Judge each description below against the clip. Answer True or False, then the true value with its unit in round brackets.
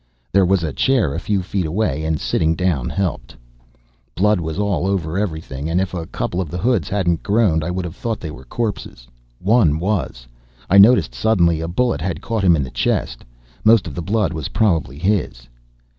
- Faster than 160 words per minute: True (200 wpm)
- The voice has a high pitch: False (90 Hz)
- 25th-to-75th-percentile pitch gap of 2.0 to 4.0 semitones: False (4.4 semitones)